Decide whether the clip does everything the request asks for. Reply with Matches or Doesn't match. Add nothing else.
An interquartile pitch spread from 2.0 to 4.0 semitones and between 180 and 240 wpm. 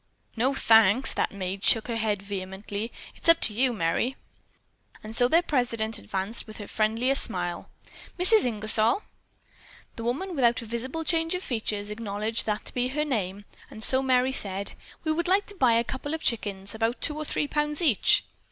Doesn't match